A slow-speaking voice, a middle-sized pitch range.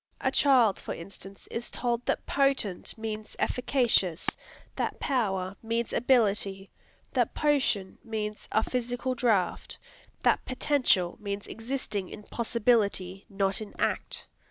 Yes: slow, 120 wpm; average, 3.9 semitones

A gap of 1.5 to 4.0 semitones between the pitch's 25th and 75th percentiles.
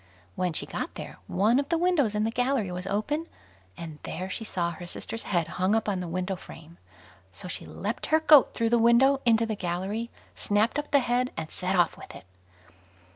No: average, 5.3 semitones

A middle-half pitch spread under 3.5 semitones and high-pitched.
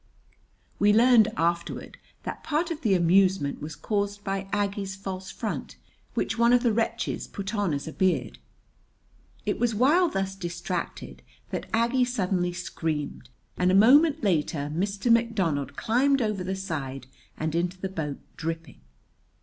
No: average, 5.0 semitones; high, 195 Hz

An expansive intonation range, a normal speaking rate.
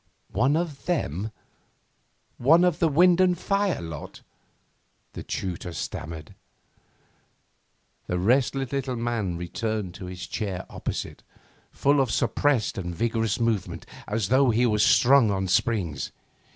No: wide, 6.7 semitones; slow, 125 wpm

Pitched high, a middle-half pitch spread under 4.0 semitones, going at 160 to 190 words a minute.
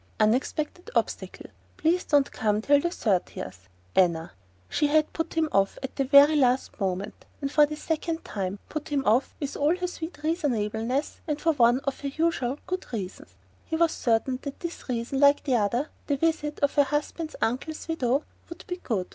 No: very high, 280 Hz; average, 5.2 semitones; average, 180 wpm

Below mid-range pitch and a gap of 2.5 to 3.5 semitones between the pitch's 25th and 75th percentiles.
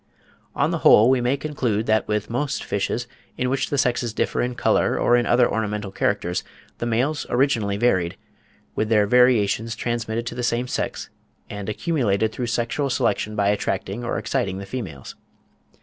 Yes: low, 115 Hz; average, 3.1 semitones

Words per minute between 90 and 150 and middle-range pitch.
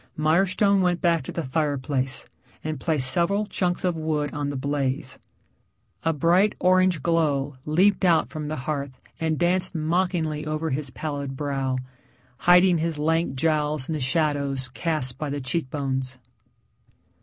Yes: average, 145 wpm; medium, 155 Hz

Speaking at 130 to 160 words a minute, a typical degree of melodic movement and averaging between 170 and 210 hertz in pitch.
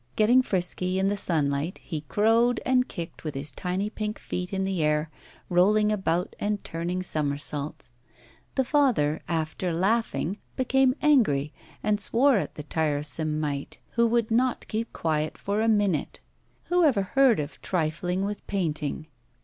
No: average, 150 wpm; wide, 6.1 semitones; medium, 185 Hz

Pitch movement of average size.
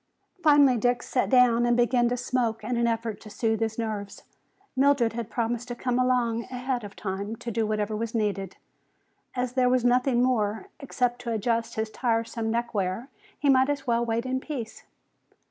No: narrow, 2.0 semitones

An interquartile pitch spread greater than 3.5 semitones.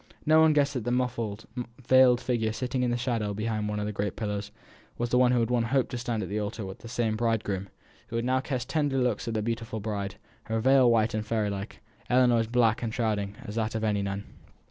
No: average, 2.8 semitones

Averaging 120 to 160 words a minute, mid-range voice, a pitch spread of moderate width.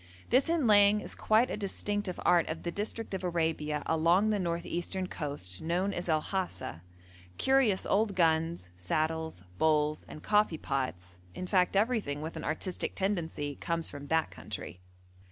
Yes: average, 155 wpm; medium, 170 Hz; average, 4.6 semitones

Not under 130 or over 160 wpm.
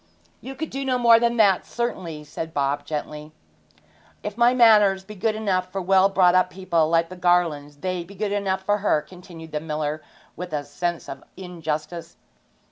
No: average, 185 wpm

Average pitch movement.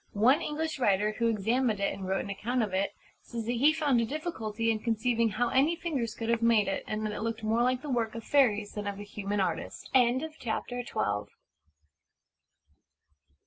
Yes: average, 3.1 semitones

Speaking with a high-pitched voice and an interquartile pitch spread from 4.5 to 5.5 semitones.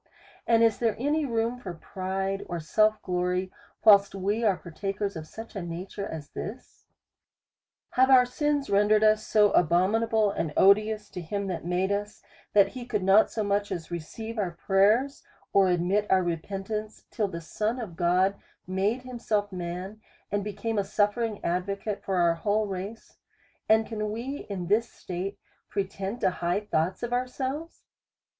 No: high, 205 Hz; average, 3.1 semitones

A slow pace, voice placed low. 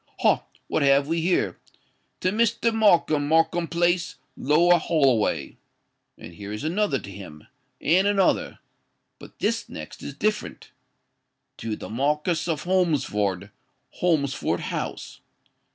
No: slow, 110 wpm; medium, 155 Hz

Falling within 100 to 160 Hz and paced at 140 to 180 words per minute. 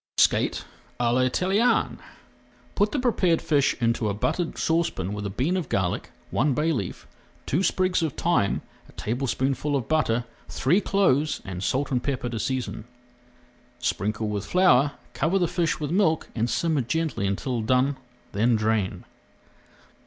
Yes: low, 135 Hz; average, 150 wpm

